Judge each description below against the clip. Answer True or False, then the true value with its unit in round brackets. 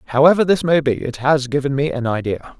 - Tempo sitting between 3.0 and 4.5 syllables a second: False (6.0 syllables/s)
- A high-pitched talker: False (140 Hz)